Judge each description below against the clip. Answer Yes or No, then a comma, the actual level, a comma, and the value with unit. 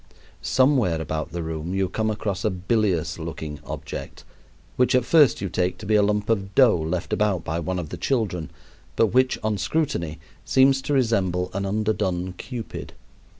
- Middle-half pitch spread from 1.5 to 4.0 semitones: No, average, 4.5 semitones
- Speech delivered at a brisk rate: No, average, 175 wpm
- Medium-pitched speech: No, low, 100 Hz